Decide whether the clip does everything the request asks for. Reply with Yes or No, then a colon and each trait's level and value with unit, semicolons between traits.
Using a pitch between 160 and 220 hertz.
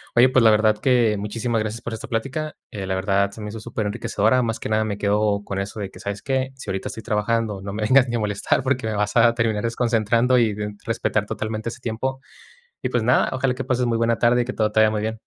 No: low, 110 Hz